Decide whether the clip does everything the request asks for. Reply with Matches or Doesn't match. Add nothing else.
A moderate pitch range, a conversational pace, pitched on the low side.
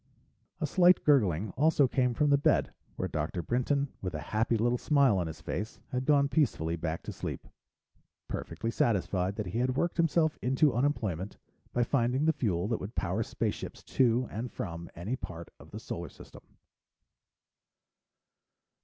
Doesn't match